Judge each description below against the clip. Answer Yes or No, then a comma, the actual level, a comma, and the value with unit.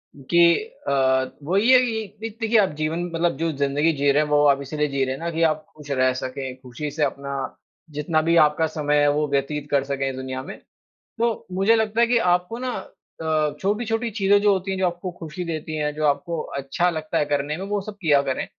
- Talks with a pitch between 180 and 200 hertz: No, medium, 155 Hz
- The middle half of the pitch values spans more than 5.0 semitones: Yes, wide, 5.4 semitones